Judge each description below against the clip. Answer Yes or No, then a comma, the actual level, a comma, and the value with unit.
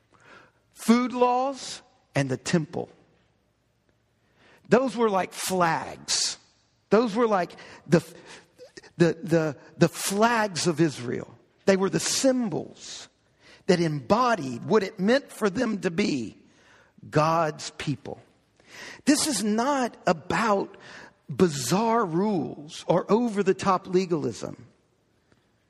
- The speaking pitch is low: No, high, 190 Hz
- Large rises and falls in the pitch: Yes, wide, 6.1 semitones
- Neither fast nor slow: No, slow, 105 wpm